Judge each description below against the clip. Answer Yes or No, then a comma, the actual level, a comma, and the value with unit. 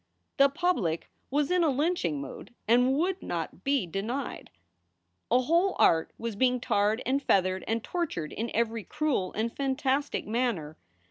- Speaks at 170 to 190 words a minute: No, average, 150 wpm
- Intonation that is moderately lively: No, wide, 6.1 semitones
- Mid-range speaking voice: No, high, 245 Hz